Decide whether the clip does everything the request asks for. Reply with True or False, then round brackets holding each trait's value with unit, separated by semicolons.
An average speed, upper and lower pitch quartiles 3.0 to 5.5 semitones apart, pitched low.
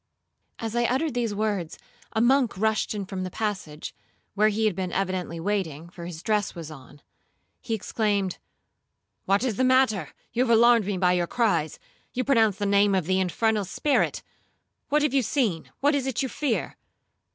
False (175 wpm; 4.3 semitones; 210 Hz)